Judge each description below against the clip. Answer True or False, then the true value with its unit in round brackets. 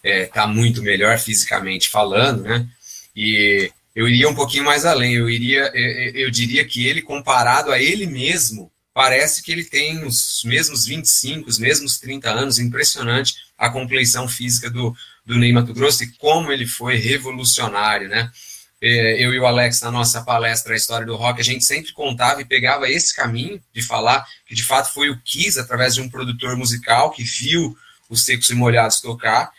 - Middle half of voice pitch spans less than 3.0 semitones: True (2.4 semitones)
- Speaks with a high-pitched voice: False (120 Hz)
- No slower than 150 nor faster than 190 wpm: True (180 wpm)